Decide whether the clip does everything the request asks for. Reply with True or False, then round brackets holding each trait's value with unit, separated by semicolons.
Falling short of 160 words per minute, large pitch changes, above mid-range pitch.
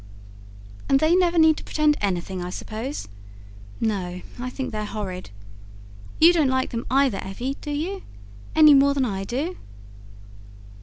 True (150 wpm; 6.8 semitones; 260 Hz)